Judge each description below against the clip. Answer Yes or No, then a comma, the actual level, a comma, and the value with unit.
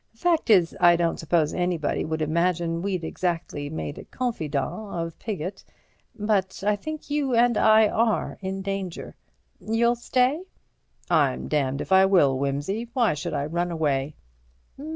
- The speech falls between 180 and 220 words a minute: No, average, 150 wpm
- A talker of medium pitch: Yes, medium, 180 Hz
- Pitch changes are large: Yes, wide, 5.7 semitones